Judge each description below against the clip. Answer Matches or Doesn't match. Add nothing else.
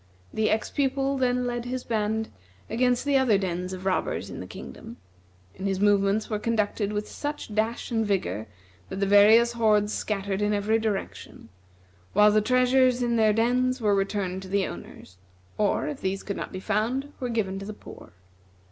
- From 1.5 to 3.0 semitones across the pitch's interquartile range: Doesn't match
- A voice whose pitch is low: Doesn't match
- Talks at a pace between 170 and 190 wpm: Matches